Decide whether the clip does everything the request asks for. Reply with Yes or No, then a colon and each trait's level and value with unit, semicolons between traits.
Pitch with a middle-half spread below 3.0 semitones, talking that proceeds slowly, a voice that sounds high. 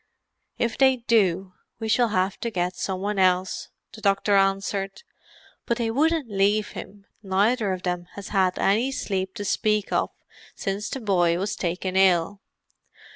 No: narrow, 2.6 semitones; average, 160 wpm; high, 200 Hz